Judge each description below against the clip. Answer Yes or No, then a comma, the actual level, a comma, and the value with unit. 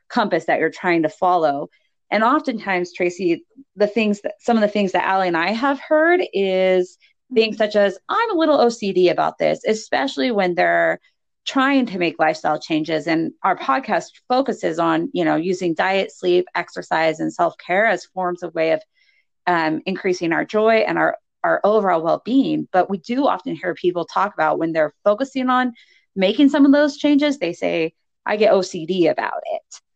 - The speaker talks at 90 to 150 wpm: No, average, 185 wpm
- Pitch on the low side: No, high, 195 Hz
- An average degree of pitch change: No, wide, 7.2 semitones